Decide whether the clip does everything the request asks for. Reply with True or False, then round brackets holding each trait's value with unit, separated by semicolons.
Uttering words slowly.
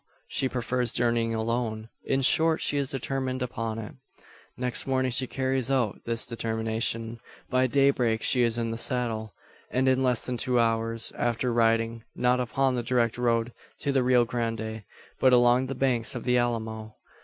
False (175 wpm)